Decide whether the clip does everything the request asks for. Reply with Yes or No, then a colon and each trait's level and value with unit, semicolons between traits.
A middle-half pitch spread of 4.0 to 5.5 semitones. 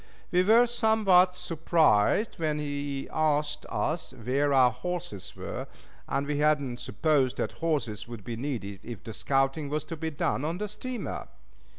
Yes: average, 4.5 semitones